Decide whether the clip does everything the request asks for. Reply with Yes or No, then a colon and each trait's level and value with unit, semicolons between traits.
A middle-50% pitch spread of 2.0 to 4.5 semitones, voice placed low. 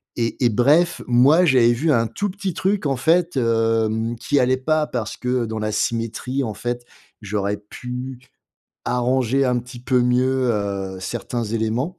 Yes: average, 2.9 semitones; low, 125 Hz